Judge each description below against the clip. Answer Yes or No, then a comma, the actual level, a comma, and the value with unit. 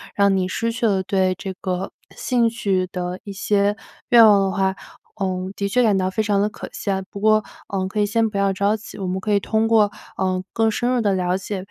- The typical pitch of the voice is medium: No, high, 200 Hz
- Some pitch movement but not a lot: No, narrow, 2.3 semitones